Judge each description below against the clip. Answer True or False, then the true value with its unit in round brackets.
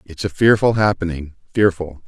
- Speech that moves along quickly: False (145 wpm)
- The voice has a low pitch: True (90 Hz)